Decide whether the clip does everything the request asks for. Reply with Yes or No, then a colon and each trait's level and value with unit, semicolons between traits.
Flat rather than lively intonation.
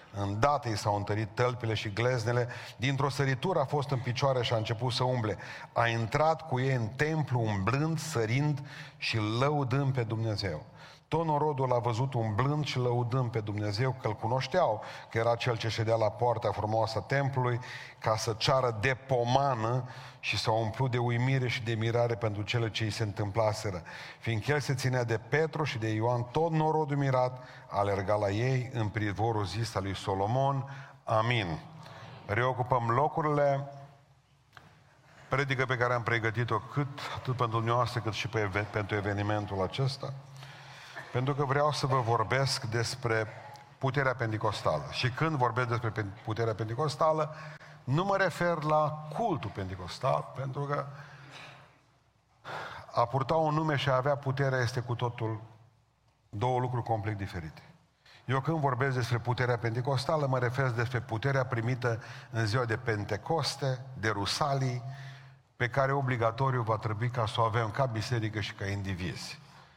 No: average, 3.6 semitones